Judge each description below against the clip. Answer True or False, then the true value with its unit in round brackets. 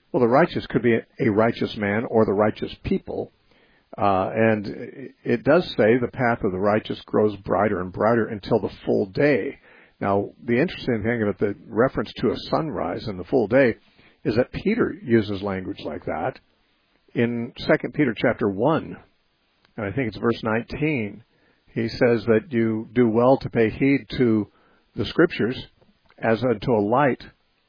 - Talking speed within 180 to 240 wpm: False (170 wpm)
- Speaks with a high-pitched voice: False (115 Hz)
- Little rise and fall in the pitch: True (2.2 semitones)